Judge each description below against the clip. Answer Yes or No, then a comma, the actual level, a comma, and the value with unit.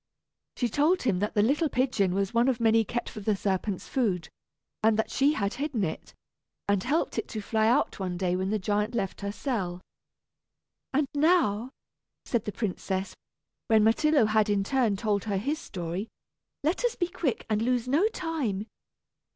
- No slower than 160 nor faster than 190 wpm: Yes, average, 180 wpm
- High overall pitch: Yes, high, 220 Hz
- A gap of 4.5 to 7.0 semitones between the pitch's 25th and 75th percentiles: Yes, average, 5.1 semitones